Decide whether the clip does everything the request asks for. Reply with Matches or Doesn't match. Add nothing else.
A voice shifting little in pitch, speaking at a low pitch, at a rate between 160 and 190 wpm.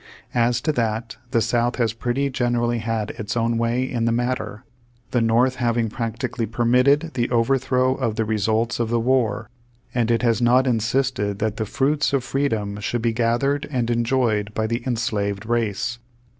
Matches